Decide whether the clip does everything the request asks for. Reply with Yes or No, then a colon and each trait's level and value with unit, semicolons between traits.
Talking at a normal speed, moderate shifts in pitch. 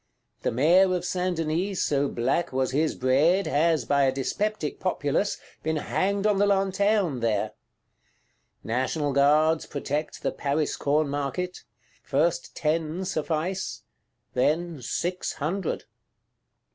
No: slow, 120 wpm; average, 4.4 semitones